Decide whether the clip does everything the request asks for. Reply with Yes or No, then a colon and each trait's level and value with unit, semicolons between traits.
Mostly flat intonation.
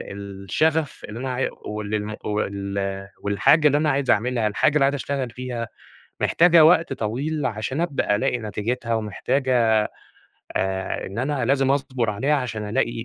No: average, 4.6 semitones